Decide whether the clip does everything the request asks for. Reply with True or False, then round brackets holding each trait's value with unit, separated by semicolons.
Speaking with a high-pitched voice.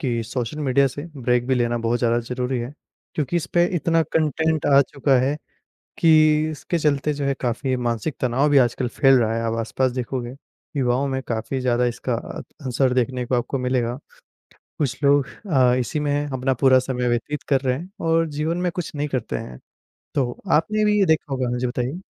False (130 Hz)